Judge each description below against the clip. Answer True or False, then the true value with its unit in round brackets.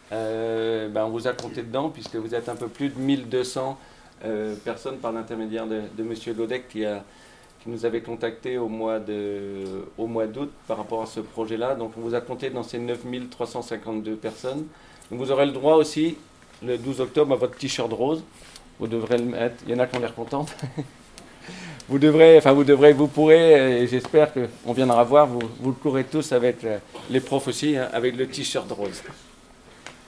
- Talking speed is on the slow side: False (200 wpm)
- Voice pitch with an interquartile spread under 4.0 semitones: True (3.3 semitones)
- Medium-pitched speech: False (120 Hz)